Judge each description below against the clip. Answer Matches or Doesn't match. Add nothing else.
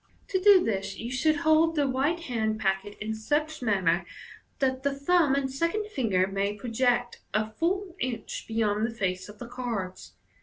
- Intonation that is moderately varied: Doesn't match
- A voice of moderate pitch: Doesn't match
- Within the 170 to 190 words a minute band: Matches